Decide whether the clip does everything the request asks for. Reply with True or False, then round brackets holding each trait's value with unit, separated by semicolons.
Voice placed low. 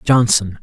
True (110 Hz)